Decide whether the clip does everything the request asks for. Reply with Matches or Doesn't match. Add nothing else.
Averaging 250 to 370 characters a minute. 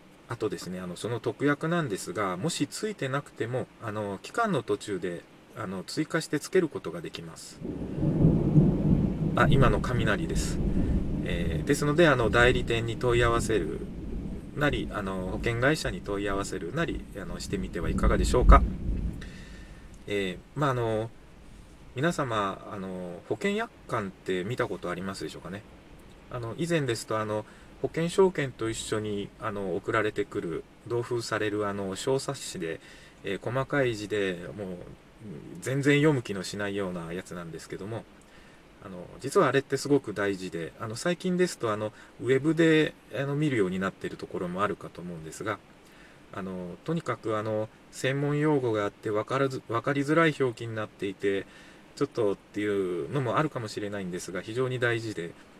Matches